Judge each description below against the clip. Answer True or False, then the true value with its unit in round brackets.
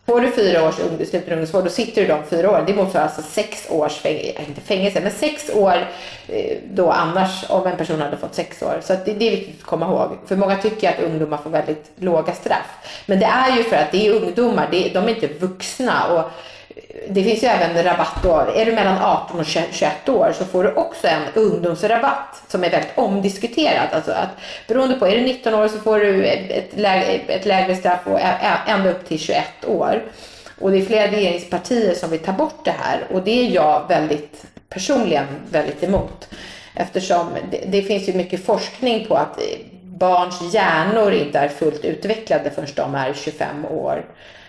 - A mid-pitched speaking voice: False (195 Hz)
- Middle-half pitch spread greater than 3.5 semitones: True (3.9 semitones)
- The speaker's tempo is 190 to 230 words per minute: True (200 wpm)